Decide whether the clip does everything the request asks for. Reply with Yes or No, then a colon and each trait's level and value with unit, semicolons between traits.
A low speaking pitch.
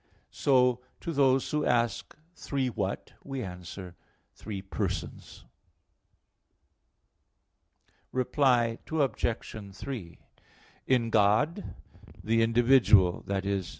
Yes: low, 115 Hz